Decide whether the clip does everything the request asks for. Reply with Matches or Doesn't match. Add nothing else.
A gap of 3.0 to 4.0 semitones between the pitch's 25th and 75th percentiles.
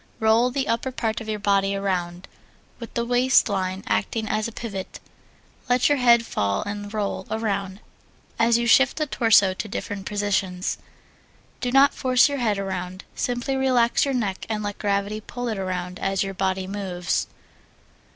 Matches